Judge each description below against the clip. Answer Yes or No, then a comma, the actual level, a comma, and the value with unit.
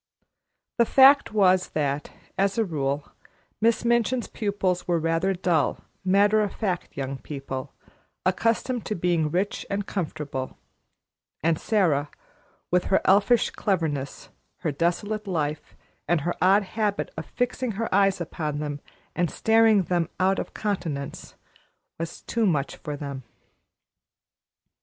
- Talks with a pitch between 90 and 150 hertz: No, medium, 180 Hz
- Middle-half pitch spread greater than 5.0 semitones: Yes, wide, 5.4 semitones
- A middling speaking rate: No, slow, 130 wpm